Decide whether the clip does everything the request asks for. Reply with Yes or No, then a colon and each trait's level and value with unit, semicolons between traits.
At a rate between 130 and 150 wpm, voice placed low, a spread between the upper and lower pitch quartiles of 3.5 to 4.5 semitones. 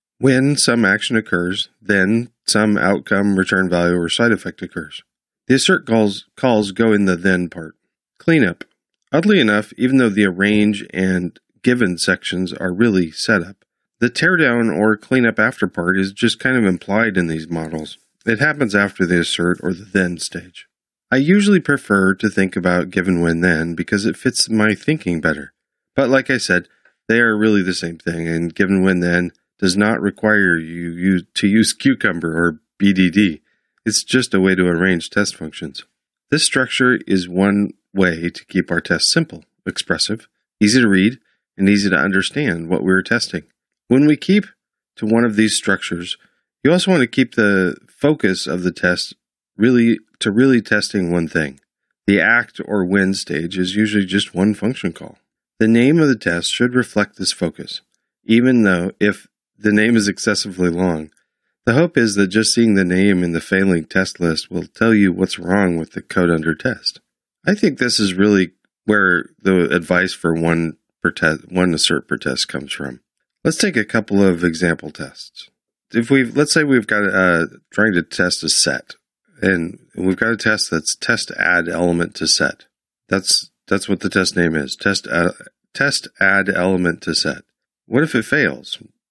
No: average, 180 wpm; very low, 95 Hz; average, 4.0 semitones